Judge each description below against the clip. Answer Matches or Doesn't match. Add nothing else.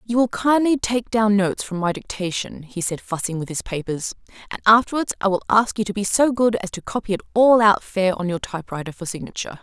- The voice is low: Doesn't match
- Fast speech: Matches